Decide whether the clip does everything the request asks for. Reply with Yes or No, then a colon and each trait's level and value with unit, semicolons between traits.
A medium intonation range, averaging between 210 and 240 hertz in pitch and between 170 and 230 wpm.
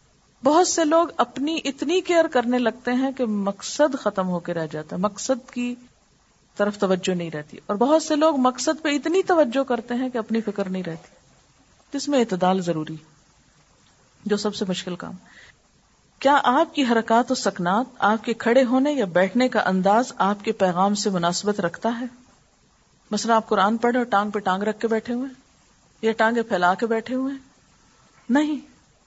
Yes: average, 4.9 semitones; high, 230 Hz; average, 180 wpm